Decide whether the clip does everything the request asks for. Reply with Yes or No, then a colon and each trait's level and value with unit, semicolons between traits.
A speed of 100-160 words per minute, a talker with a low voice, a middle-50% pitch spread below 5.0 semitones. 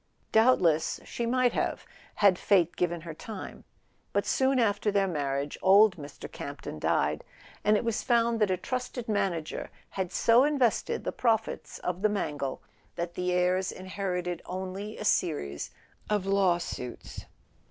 No: average, 150 wpm; high, 190 Hz; average, 4.2 semitones